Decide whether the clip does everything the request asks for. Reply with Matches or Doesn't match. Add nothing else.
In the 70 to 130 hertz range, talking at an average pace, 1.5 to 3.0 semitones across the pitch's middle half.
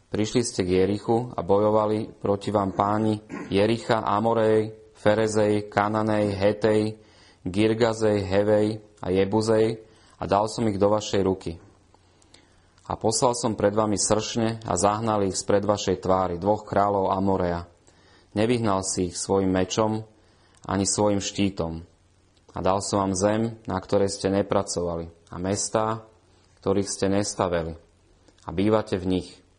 Matches